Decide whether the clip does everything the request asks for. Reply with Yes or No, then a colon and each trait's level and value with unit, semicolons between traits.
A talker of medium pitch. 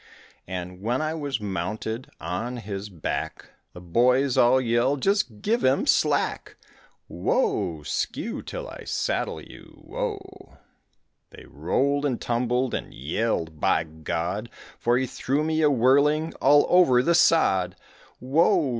No: low, 125 Hz